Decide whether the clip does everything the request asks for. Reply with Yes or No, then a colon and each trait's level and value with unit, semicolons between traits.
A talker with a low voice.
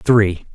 Yes: low, 100 Hz